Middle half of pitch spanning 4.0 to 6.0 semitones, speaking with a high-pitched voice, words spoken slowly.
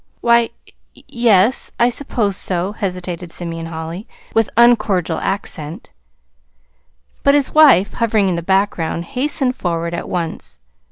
Yes: wide, 5.6 semitones; high, 195 Hz; slow, 125 wpm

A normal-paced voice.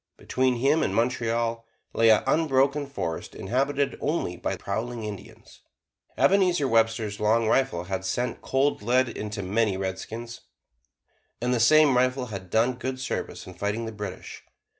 Yes: average, 150 wpm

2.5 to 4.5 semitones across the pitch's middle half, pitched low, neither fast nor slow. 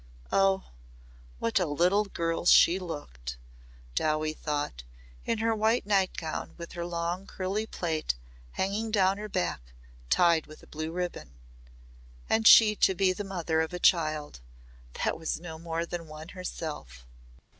No: average, 3.7 semitones; medium, 170 Hz; average, 150 wpm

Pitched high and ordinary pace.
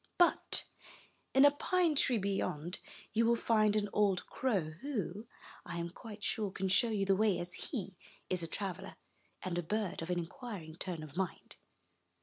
Yes: high, 195 Hz; average, 175 wpm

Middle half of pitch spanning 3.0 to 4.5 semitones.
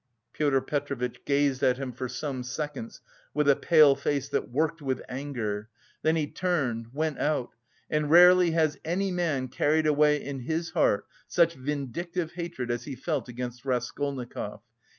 Yes: average, 3.7 semitones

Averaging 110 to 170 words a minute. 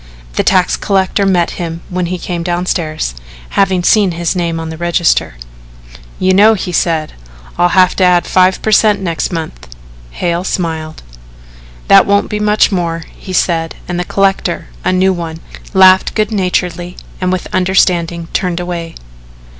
Yes: average, 160 wpm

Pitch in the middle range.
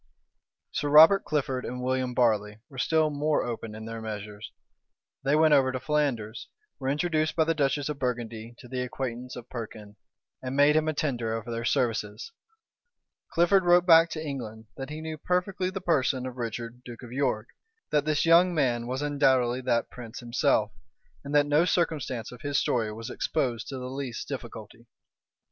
No: low, 130 Hz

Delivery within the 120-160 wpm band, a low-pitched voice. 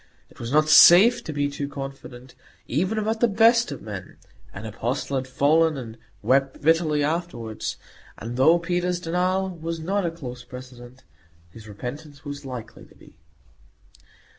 No: average, 155 wpm; medium, 145 Hz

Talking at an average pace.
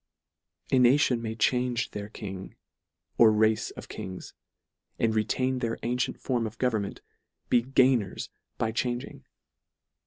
No: slow, 130 wpm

